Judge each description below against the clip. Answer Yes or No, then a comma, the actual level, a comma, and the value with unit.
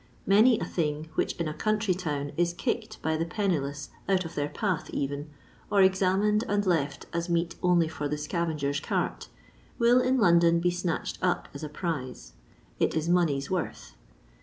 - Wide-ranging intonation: No, average, 3.9 semitones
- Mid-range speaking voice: Yes, medium, 170 Hz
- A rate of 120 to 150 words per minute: No, average, 175 wpm